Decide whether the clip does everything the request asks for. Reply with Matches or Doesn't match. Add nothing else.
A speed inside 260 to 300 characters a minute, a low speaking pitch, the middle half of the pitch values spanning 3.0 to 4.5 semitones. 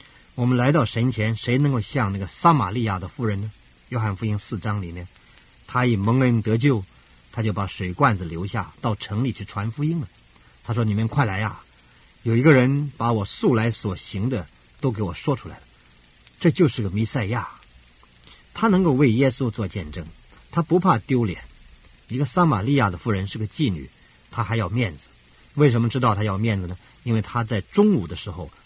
Doesn't match